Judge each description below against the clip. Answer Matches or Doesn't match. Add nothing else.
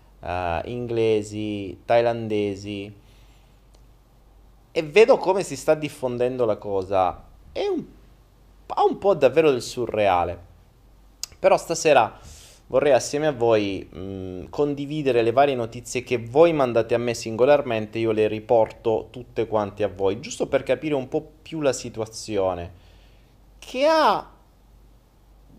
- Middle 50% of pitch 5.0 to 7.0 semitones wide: Matches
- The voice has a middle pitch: Doesn't match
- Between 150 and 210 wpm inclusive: Doesn't match